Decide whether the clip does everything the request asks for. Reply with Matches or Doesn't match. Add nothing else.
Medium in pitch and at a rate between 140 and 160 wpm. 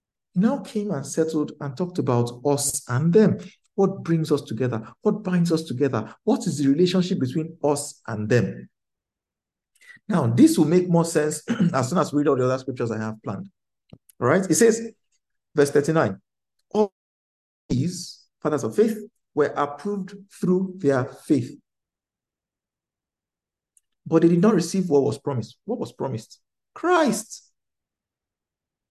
Matches